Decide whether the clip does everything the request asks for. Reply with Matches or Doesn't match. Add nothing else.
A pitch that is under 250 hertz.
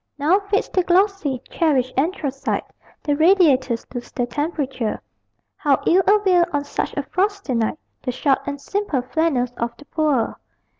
Doesn't match